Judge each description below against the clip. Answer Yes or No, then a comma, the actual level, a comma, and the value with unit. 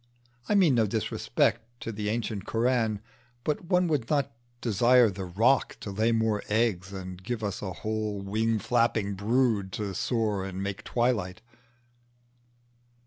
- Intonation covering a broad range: No, average, 3.1 semitones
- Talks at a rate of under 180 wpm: Yes, average, 145 wpm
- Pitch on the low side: Yes, low, 110 Hz